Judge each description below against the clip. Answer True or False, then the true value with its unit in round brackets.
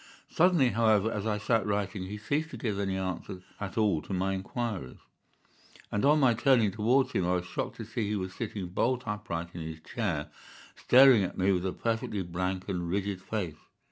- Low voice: True (105 Hz)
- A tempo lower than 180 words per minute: False (205 wpm)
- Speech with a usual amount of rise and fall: True (3.6 semitones)